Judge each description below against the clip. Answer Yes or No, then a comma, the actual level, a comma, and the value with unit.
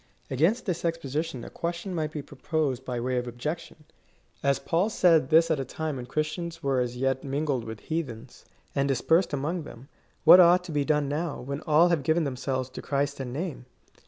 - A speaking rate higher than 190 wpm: Yes, fast, 205 wpm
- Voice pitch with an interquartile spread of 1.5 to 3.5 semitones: No, average, 4.0 semitones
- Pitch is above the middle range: No, medium, 150 Hz